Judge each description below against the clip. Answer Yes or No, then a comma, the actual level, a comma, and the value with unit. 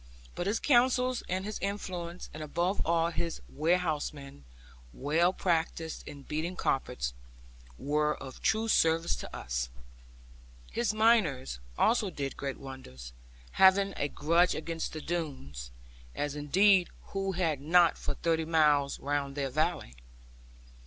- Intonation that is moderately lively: Yes, average, 4.5 semitones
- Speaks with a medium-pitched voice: Yes, medium, 160 Hz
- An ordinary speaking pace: No, slow, 130 wpm